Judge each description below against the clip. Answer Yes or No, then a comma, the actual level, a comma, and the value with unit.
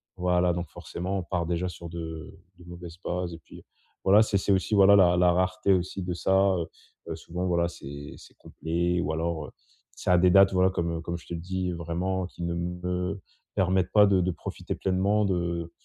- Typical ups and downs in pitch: No, narrow, 1.6 semitones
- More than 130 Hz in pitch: No, very low, 90 Hz